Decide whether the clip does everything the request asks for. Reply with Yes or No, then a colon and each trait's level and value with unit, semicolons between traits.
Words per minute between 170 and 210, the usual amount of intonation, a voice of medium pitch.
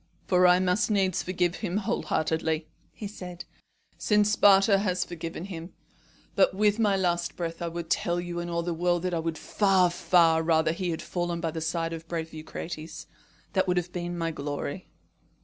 No: average, 190 wpm; narrow, 2.1 semitones; medium, 175 Hz